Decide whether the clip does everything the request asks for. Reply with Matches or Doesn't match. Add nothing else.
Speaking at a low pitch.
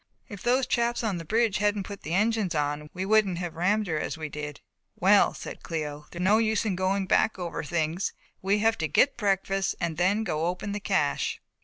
Doesn't match